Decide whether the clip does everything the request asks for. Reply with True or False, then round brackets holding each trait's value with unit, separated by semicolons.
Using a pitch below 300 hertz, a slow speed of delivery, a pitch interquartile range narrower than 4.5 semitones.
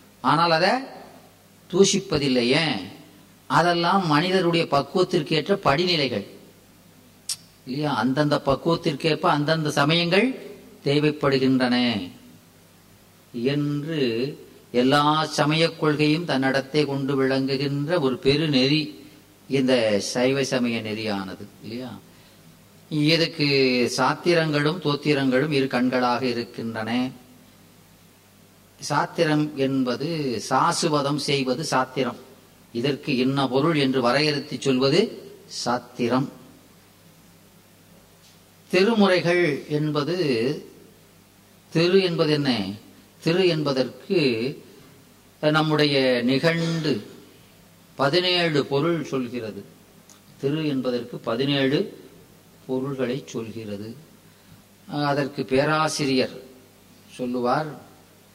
True (135 Hz; 65 wpm; 3.6 semitones)